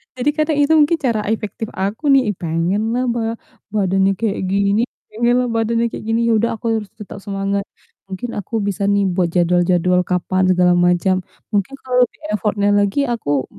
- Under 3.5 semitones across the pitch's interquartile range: No, average, 3.8 semitones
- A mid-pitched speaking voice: No, high, 205 Hz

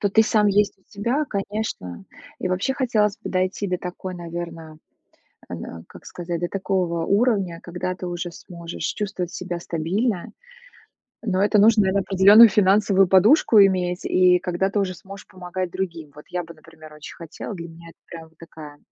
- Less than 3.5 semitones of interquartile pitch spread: Yes, average, 2.9 semitones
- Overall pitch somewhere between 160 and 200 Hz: Yes, medium, 185 Hz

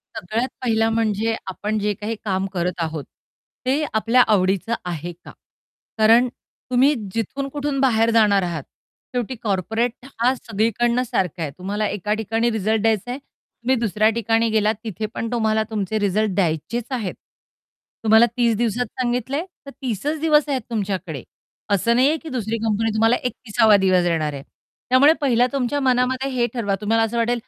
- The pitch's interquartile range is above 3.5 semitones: No, average, 3.2 semitones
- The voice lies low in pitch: No, high, 225 Hz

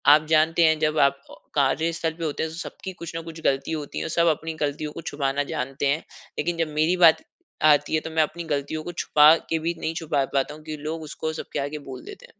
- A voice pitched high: No, medium, 155 Hz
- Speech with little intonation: Yes, narrow, 2.0 semitones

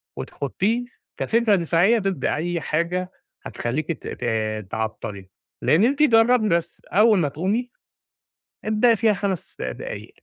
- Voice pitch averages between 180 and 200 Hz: Yes, medium, 185 Hz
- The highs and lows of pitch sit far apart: Yes, wide, 6.6 semitones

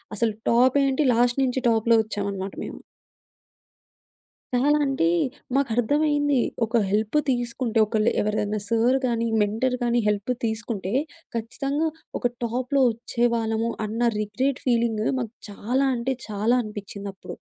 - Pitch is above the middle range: Yes, high, 235 Hz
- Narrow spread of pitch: No, average, 3.0 semitones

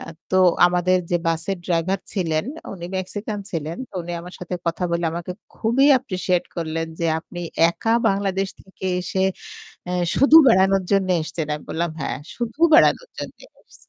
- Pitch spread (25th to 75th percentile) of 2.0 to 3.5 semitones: Yes, narrow, 2.5 semitones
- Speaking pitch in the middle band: Yes, medium, 180 Hz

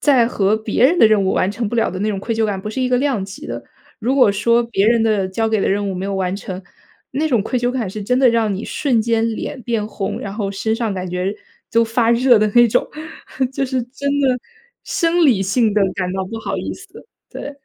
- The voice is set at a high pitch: Yes, high, 225 Hz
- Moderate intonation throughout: Yes, average, 3.7 semitones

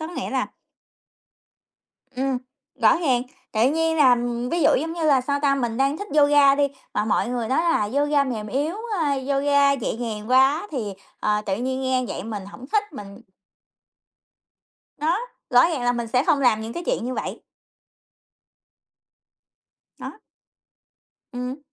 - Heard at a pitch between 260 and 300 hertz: Yes, very high, 265 Hz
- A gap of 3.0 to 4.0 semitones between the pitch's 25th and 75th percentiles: Yes, average, 3.4 semitones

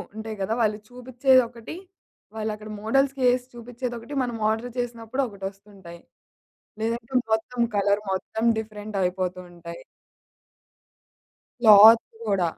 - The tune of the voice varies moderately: Yes, average, 3.1 semitones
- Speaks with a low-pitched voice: No, high, 220 Hz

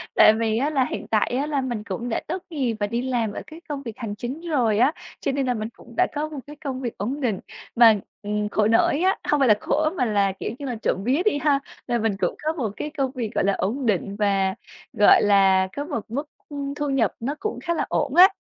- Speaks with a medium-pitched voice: No, high, 245 Hz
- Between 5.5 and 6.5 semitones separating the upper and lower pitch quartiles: No, average, 5.1 semitones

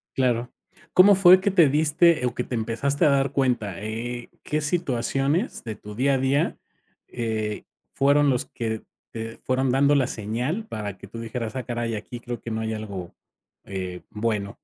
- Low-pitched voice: Yes, low, 120 Hz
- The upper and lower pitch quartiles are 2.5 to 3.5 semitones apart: No, average, 4.1 semitones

